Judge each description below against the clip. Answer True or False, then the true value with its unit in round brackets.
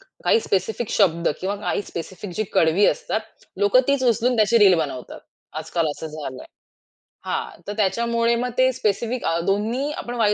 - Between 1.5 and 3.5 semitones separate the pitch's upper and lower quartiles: False (4.5 semitones)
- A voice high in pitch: True (215 Hz)